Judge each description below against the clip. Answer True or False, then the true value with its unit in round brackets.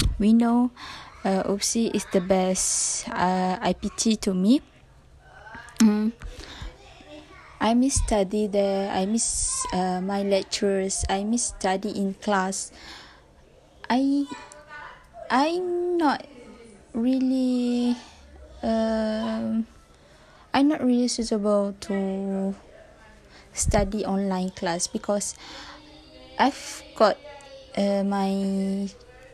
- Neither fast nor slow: False (90 wpm)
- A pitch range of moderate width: True (3.9 semitones)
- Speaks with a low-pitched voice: False (215 Hz)